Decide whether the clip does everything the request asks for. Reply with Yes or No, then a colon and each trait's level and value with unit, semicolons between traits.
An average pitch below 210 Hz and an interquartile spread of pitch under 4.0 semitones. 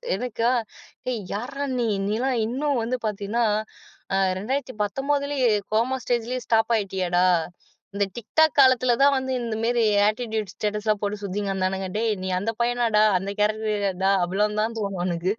No: high, 220 Hz; average, 3.4 semitones